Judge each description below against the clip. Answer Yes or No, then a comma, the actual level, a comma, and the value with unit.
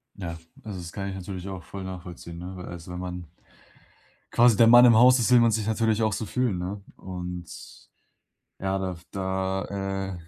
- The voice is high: No, very low, 95 Hz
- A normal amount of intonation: Yes, average, 3.4 semitones